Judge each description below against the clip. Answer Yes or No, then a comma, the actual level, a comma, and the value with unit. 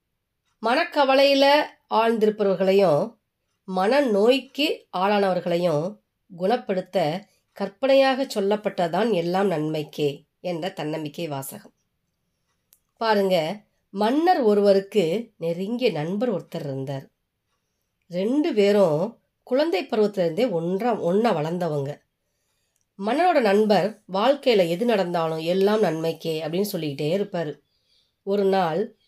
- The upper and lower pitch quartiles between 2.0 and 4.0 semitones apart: No, average, 5.0 semitones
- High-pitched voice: Yes, high, 195 Hz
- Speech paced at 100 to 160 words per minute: No, average, 80 wpm